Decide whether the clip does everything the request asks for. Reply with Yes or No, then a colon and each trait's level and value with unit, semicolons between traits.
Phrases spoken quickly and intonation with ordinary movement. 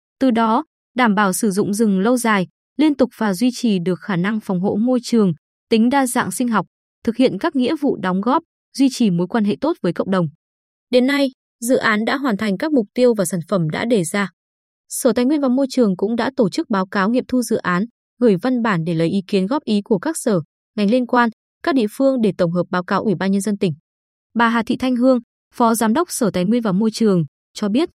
Yes: fast, 255 wpm; average, 4.2 semitones